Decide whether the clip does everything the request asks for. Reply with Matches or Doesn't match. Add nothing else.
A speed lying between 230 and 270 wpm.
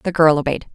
Matches